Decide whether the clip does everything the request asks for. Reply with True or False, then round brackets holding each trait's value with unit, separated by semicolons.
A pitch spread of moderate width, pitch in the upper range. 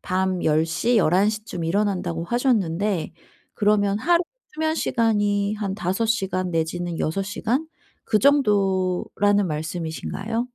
True (3.7 semitones; 200 Hz)